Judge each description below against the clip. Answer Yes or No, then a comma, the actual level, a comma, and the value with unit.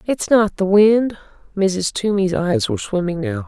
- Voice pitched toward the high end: Yes, high, 200 Hz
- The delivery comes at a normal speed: Yes, average, 175 wpm